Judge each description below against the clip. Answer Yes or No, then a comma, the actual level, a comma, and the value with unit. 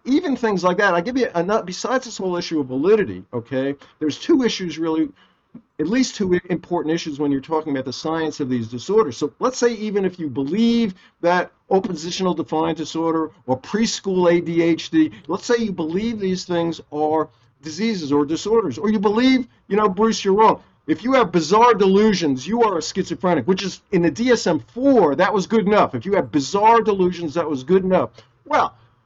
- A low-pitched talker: No, medium, 180 Hz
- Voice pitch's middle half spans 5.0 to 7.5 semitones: Yes, wide, 5.6 semitones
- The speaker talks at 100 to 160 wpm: No, average, 195 wpm